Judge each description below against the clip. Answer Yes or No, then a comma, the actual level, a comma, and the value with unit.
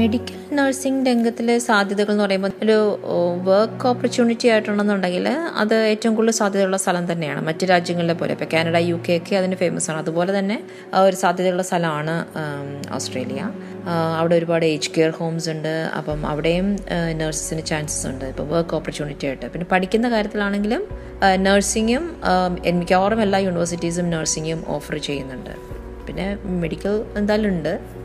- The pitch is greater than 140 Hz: Yes, medium, 185 Hz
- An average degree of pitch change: Yes, average, 4.0 semitones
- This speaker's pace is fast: Yes, fast, 135 wpm